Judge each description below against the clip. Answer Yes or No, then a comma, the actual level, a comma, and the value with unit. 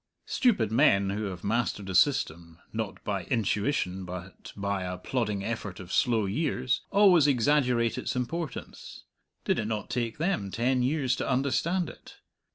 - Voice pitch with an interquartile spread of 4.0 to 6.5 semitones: Yes, wide, 5.4 semitones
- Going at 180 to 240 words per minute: No, average, 155 wpm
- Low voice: Yes, low, 115 Hz